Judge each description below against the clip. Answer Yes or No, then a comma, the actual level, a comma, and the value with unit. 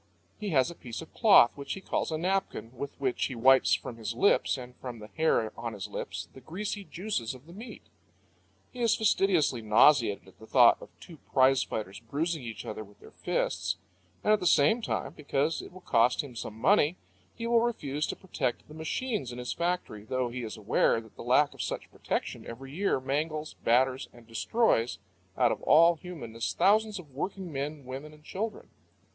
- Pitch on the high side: No, medium, 140 Hz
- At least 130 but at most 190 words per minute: No, average, 200 wpm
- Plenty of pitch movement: Yes, wide, 6.9 semitones